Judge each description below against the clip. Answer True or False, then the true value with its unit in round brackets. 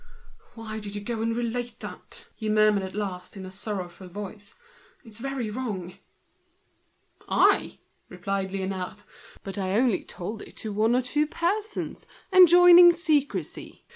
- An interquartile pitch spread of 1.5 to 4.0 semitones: False (4.5 semitones)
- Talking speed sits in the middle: True (150 wpm)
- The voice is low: False (215 Hz)